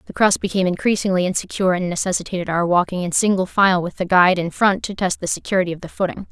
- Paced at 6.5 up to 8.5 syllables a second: Yes, 7.0 syllables/s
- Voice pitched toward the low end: No, medium, 185 Hz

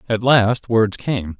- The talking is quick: No, average, 170 wpm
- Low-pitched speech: Yes, low, 110 Hz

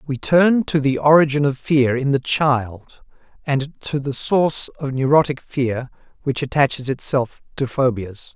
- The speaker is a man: Yes, male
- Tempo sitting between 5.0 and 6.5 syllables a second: No, 4.4 syllables/s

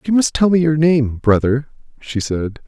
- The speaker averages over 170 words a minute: Yes, average, 200 wpm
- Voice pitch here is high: No, medium, 140 Hz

